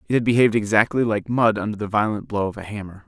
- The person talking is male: Yes, male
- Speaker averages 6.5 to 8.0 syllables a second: Yes, 6.7 syllables/s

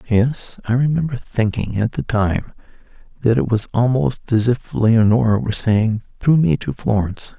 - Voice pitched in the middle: No, low, 115 Hz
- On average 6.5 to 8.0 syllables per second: No, 4.7 syllables/s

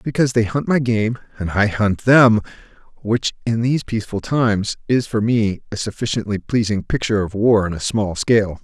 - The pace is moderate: Yes, average, 180 wpm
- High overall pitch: No, low, 110 Hz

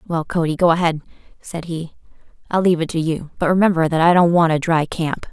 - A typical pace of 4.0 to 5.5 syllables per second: No, 6.0 syllables/s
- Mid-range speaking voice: Yes, medium, 165 Hz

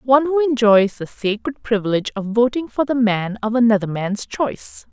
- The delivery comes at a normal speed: Yes, average, 185 wpm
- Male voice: No, female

